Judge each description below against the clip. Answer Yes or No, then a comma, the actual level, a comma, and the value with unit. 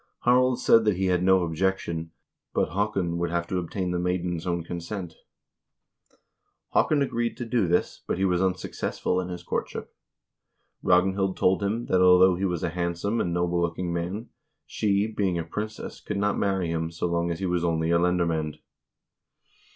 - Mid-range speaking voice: No, very low, 90 Hz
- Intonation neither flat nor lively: No, narrow, 2.3 semitones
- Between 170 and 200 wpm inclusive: Yes, average, 180 wpm